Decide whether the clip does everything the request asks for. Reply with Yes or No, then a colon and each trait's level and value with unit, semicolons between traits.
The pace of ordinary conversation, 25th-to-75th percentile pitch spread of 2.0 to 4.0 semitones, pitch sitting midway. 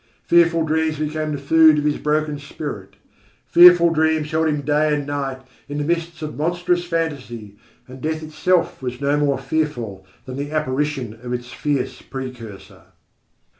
Yes: average, 160 wpm; average, 2.9 semitones; medium, 150 Hz